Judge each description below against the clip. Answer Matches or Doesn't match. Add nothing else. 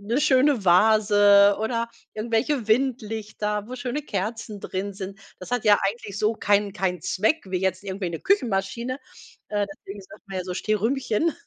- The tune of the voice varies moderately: Matches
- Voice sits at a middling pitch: Doesn't match